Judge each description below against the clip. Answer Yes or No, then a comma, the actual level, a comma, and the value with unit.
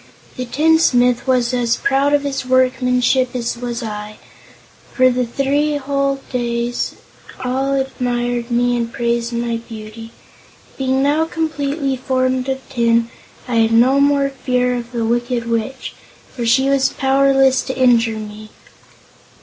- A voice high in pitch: Yes, very high, 250 Hz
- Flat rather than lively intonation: Yes, narrow, 2.3 semitones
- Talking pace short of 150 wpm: Yes, average, 140 wpm